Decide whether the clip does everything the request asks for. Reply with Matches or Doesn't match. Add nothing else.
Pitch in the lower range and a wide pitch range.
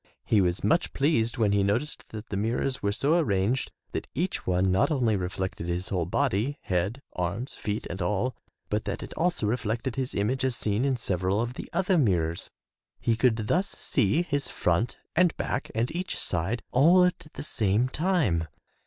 Matches